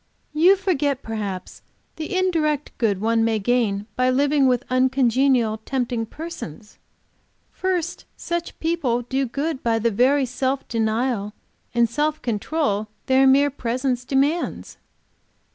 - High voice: Yes, very high, 255 Hz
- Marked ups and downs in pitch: No, average, 4.3 semitones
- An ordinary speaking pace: No, slow, 125 wpm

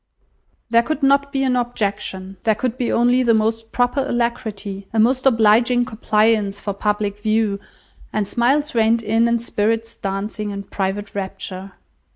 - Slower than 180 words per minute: Yes, average, 155 wpm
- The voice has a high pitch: Yes, high, 225 Hz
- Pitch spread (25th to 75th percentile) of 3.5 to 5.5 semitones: No, average, 2.9 semitones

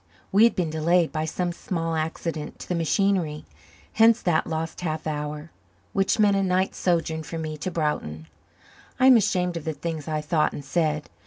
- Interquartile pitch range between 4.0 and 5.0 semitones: No, average, 2.8 semitones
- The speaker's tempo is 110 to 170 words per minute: No, average, 185 wpm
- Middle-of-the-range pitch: Yes, medium, 165 Hz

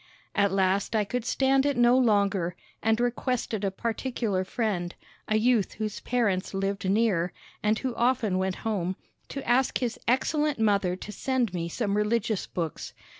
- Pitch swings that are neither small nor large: Yes, average, 4.0 semitones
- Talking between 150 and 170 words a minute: Yes, average, 160 wpm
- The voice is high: Yes, high, 215 Hz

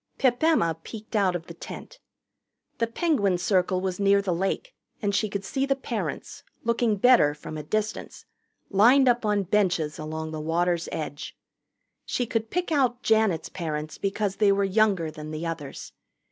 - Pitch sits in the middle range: No, high, 195 Hz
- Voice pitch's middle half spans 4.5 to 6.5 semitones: Yes, average, 5.3 semitones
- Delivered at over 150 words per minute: Yes, average, 170 wpm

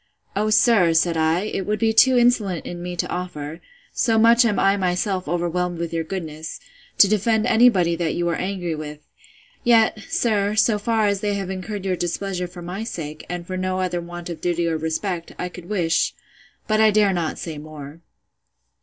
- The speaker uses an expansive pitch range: No, average, 3.7 semitones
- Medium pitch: Yes, medium, 180 Hz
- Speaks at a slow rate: No, average, 195 wpm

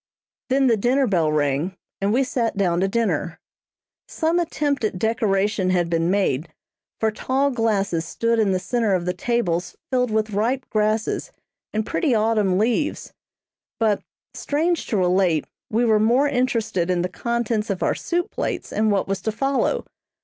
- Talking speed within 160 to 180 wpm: Yes, average, 165 wpm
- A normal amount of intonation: Yes, average, 4.5 semitones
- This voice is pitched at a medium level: No, high, 215 Hz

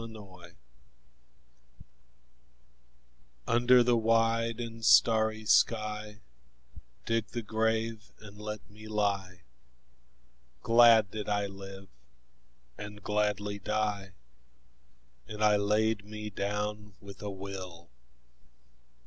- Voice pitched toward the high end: No, low, 105 Hz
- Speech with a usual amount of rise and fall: No, narrow, 1.7 semitones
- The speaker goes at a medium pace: No, slow, 90 wpm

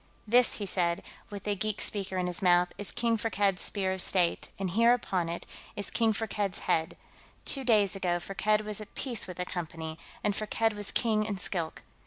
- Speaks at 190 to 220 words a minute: Yes, average, 200 wpm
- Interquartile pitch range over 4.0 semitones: No, average, 3.0 semitones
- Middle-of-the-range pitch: No, high, 200 Hz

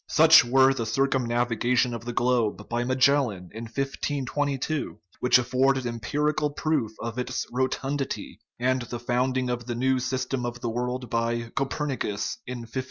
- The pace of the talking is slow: No, average, 155 wpm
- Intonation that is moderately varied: No, narrow, 2.1 semitones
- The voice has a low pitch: Yes, low, 125 Hz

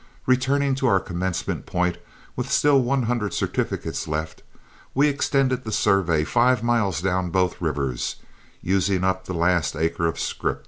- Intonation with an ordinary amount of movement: No, wide, 6.7 semitones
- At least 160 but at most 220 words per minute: No, average, 150 wpm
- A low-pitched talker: Yes, very low, 95 Hz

